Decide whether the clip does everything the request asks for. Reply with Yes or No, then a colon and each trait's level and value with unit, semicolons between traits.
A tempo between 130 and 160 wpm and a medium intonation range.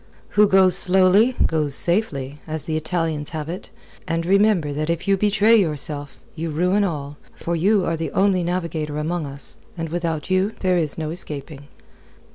No: average, 170 wpm; average, 3.6 semitones